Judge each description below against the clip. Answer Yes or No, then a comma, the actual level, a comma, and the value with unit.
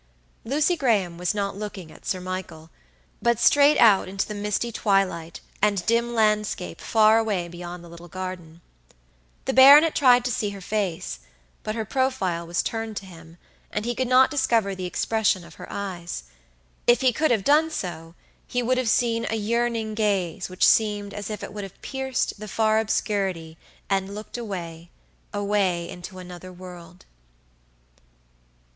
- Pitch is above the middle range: Yes, high, 205 Hz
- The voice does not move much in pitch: No, average, 4.3 semitones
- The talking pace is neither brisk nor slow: Yes, average, 165 wpm